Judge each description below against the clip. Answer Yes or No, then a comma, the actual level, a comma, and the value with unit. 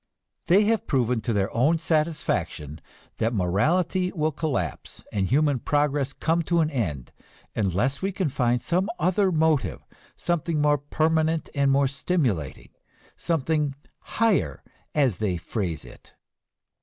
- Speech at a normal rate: No, slow, 130 wpm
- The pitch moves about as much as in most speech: No, wide, 6.0 semitones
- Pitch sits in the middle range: Yes, medium, 145 Hz